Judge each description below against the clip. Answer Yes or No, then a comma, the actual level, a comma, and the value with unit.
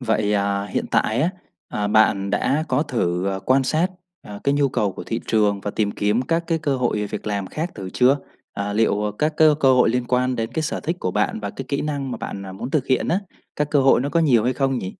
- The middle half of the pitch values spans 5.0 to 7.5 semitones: Yes, wide, 5.5 semitones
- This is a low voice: Yes, low, 120 Hz